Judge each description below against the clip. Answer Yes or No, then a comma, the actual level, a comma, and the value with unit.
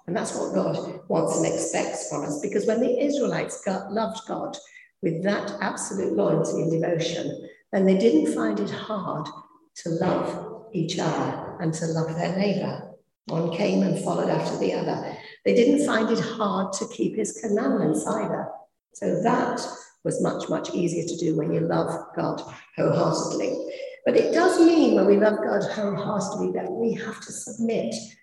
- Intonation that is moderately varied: Yes, average, 5.0 semitones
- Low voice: No, high, 210 Hz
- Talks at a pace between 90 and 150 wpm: No, average, 170 wpm